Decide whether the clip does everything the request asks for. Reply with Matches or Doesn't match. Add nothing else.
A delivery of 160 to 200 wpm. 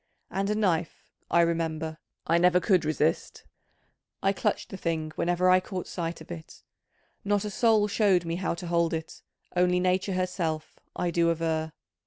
Matches